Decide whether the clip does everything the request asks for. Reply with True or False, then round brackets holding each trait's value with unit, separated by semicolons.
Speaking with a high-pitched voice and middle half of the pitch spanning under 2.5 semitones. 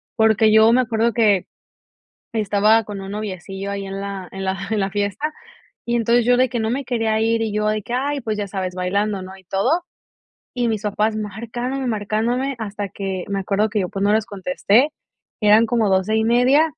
False (215 Hz; 2.8 semitones)